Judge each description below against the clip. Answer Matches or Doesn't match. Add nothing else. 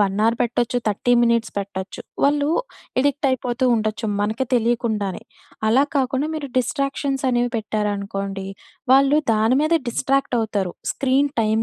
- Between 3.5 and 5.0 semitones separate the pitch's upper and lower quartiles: Matches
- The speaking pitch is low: Doesn't match